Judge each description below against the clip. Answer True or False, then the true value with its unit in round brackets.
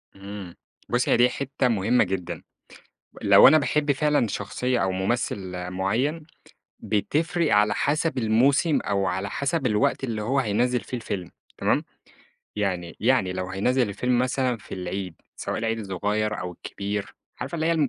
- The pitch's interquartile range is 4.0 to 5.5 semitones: True (5.1 semitones)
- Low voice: True (110 Hz)